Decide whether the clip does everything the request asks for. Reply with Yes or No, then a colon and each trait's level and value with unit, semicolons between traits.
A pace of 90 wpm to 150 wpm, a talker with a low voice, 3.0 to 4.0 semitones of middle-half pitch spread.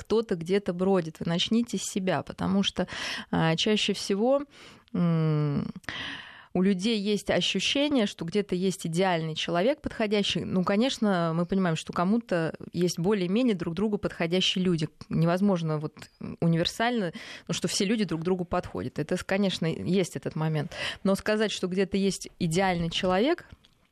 No: average, 145 wpm; medium, 185 Hz; average, 3.3 semitones